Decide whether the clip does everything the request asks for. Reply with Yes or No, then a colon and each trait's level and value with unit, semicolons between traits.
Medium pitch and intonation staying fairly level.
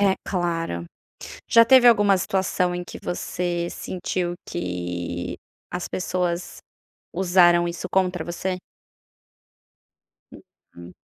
Yes: medium, 175 Hz; narrow, 1.7 semitones